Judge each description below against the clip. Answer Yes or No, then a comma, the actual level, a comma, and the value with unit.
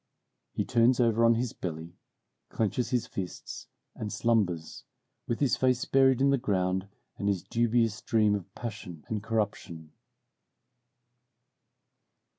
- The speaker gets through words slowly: Yes, slow, 125 wpm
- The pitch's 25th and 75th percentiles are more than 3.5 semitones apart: Yes, average, 4.0 semitones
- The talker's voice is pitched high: No, low, 110 Hz